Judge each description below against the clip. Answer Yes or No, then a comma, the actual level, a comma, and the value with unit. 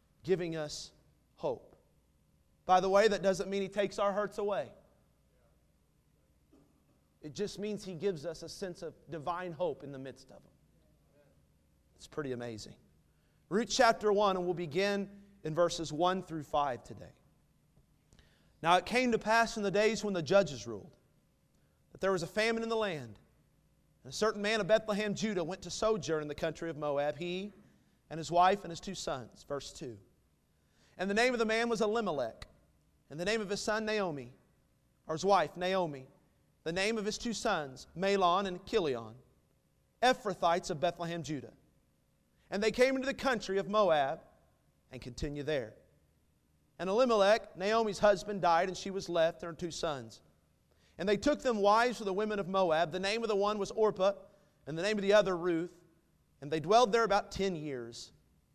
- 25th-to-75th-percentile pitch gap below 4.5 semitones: No, average, 5.0 semitones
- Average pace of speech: Yes, average, 180 wpm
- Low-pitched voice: No, medium, 185 Hz